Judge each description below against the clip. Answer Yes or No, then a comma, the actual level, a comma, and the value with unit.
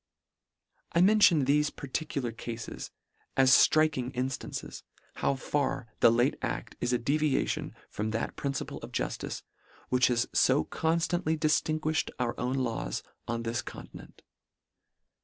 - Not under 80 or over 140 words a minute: Yes, slow, 135 wpm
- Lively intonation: No, average, 4.2 semitones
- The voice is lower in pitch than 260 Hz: Yes, low, 135 Hz